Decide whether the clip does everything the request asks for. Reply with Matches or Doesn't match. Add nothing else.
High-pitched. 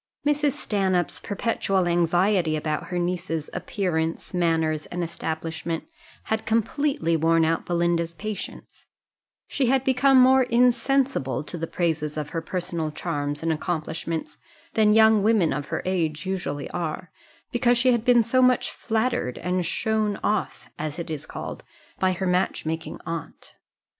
Doesn't match